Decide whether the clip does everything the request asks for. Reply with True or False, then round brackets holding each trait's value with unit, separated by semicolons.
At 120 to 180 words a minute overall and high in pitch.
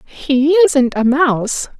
True (135 wpm; 280 Hz)